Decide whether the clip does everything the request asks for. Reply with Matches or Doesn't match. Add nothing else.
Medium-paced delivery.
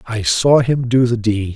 Doesn't match